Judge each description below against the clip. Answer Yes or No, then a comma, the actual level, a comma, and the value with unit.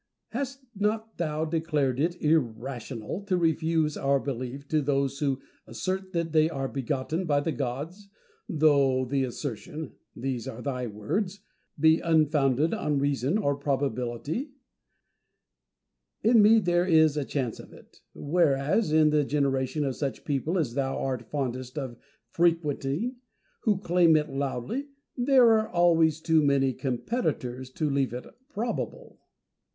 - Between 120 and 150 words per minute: Yes, average, 140 wpm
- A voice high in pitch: No, medium, 150 Hz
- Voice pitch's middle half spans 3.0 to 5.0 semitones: Yes, average, 4.1 semitones